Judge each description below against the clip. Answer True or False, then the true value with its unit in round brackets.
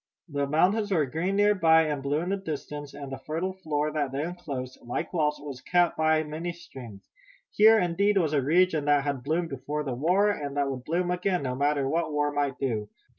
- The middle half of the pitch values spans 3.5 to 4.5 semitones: True (3.9 semitones)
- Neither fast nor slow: False (215 wpm)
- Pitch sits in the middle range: True (150 Hz)